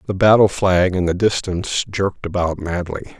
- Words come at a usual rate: Yes, average, 170 wpm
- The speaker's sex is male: Yes, male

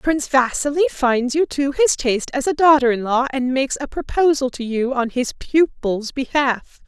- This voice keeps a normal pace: Yes, average, 190 wpm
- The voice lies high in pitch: Yes, very high, 270 Hz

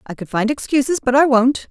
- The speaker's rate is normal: No, fast, 245 wpm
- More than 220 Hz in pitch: Yes, very high, 255 Hz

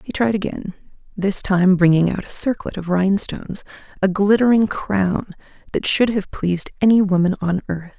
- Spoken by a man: No, female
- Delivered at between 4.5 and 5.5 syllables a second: Yes, 5.0 syllables/s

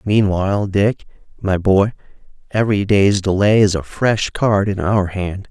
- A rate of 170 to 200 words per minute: No, average, 155 wpm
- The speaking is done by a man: Yes, male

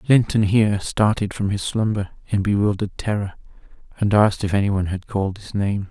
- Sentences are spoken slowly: No, average, 185 wpm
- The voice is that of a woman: No, male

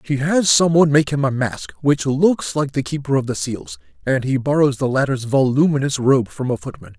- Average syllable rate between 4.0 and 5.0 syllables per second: No, 5.2 syllables/s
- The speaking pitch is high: No, low, 130 Hz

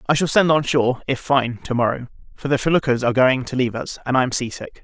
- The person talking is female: No, male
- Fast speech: Yes, fast, 275 wpm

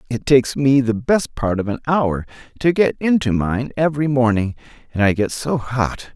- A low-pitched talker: Yes, low, 125 Hz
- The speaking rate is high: No, average, 195 wpm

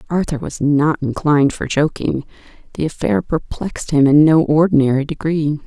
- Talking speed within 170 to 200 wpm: No, average, 150 wpm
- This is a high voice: No, medium, 145 Hz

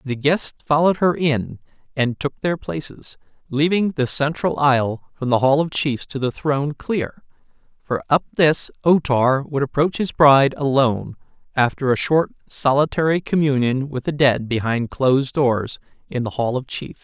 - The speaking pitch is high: No, medium, 140 Hz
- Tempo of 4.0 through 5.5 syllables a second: Yes, 4.6 syllables/s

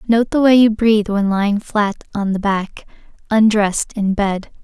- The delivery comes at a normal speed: Yes, average, 180 wpm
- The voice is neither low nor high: No, high, 210 Hz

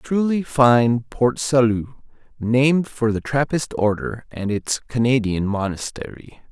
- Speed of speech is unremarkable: No, slow, 120 wpm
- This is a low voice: Yes, low, 120 Hz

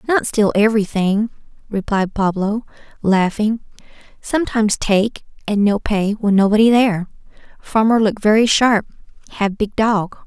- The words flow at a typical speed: No, slow, 125 wpm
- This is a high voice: Yes, high, 210 Hz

